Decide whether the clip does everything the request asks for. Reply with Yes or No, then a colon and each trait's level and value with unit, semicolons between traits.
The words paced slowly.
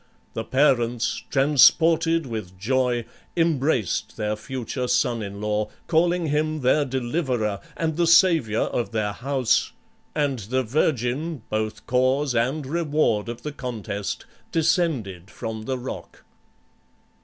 Yes: slow, 120 wpm